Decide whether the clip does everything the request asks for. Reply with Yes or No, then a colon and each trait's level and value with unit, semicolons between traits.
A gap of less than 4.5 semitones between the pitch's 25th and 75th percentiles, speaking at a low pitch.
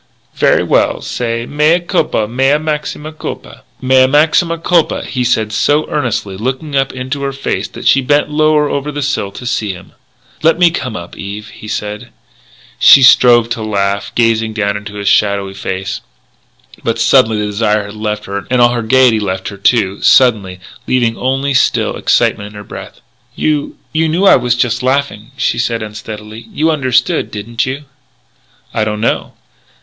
No: average, 4.9 semitones; low, 120 Hz